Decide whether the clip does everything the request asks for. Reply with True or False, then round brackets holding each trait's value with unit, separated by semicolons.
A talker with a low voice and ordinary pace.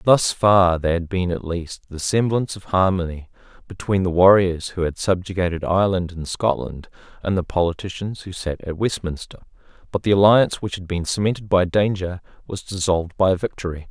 True (95 Hz; 175 wpm)